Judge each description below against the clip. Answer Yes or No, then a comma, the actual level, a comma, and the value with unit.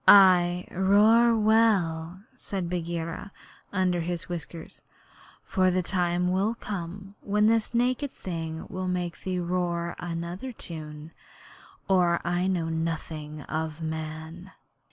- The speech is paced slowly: Yes, slow, 115 wpm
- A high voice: No, medium, 175 Hz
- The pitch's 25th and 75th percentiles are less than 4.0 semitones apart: Yes, narrow, 2.6 semitones